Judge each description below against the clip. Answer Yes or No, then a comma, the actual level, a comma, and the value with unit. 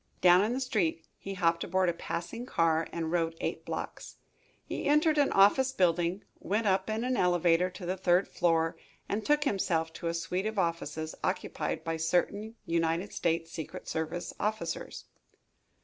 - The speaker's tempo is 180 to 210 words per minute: No, average, 165 wpm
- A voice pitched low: No, medium, 180 Hz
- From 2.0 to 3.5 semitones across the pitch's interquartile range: No, average, 4.1 semitones